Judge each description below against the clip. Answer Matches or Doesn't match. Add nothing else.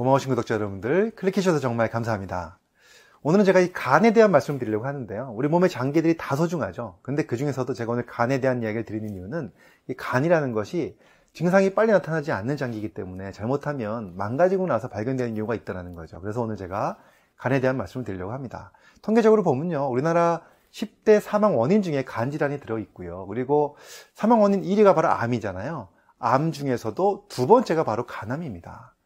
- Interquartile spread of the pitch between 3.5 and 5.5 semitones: Doesn't match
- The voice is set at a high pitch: Doesn't match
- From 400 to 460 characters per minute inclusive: Matches